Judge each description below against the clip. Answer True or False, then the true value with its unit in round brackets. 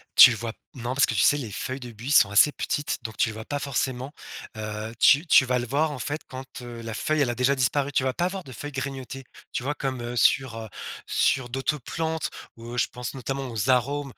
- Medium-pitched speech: False (130 Hz)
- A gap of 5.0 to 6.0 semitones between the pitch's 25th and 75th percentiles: False (3.0 semitones)